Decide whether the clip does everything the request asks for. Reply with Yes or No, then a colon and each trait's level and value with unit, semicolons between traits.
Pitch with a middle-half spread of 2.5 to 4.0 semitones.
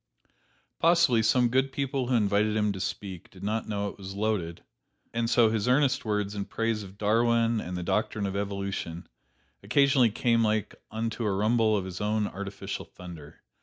Yes: average, 2.9 semitones